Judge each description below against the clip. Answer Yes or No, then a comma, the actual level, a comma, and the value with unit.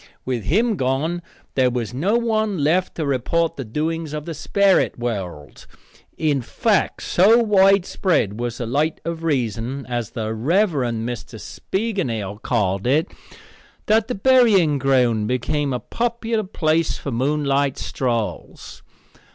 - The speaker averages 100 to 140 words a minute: Yes, slow, 135 wpm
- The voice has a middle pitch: Yes, medium, 145 Hz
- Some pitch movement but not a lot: No, wide, 7.7 semitones